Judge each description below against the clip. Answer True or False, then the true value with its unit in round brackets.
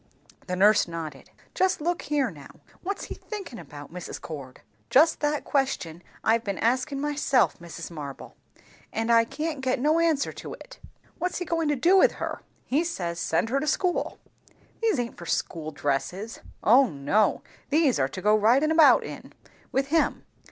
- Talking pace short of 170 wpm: False (175 wpm)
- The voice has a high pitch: True (250 Hz)